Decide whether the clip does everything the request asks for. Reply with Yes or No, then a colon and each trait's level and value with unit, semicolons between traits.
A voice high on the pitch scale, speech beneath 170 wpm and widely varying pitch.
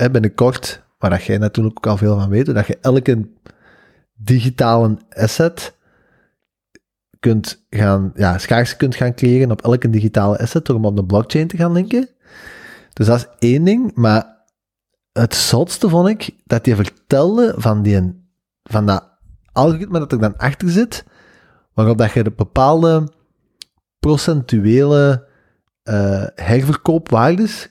No: low, 120 Hz; average, 140 wpm; wide, 6.6 semitones